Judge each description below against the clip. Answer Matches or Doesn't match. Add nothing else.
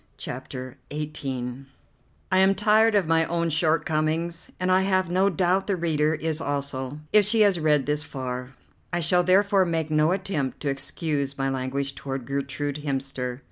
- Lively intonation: Doesn't match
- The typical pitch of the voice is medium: Matches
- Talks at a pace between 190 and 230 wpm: Doesn't match